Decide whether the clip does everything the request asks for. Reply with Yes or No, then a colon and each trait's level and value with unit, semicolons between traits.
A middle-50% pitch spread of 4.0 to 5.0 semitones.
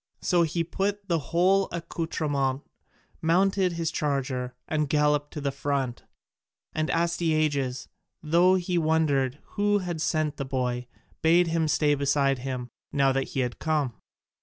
No: average, 3.6 semitones